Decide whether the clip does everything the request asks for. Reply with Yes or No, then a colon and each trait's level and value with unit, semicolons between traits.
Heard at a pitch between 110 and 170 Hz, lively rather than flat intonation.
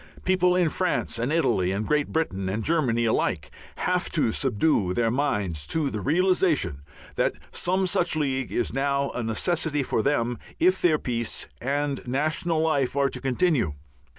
Yes: medium, 140 Hz; wide, 5.8 semitones